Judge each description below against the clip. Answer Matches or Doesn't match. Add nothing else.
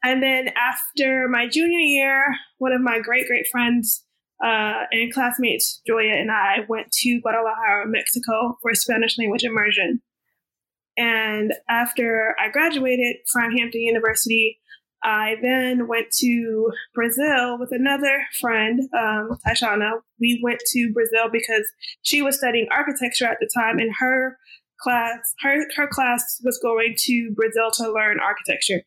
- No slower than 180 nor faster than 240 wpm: Doesn't match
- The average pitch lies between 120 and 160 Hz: Doesn't match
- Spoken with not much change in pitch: Matches